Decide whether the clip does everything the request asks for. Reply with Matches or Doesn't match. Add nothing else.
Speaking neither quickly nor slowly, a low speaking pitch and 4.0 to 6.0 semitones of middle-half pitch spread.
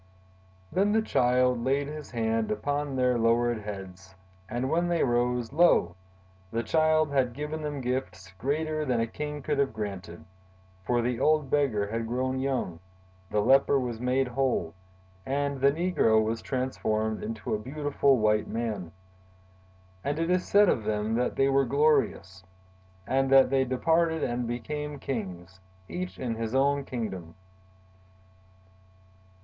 Matches